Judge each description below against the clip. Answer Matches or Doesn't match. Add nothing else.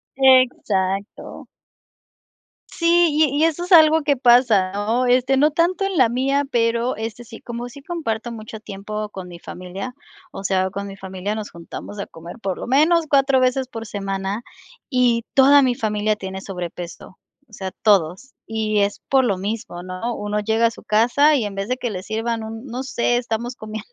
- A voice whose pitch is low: Doesn't match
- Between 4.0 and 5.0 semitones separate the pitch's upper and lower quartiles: Matches